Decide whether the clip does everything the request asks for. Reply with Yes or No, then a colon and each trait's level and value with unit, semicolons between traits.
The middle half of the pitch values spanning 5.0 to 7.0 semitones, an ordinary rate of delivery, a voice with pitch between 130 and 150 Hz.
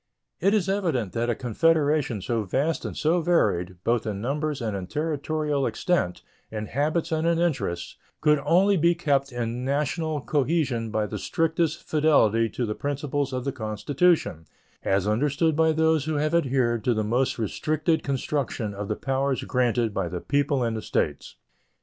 Yes: wide, 5.6 semitones; average, 170 wpm; medium, 140 Hz